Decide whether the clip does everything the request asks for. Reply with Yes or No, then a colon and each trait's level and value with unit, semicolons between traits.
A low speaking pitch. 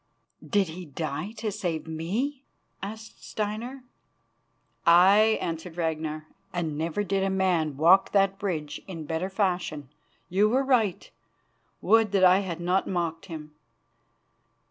No: medium, 185 Hz